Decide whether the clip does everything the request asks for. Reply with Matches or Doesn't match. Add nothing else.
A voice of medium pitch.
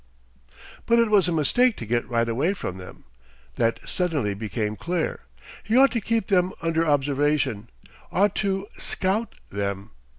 Matches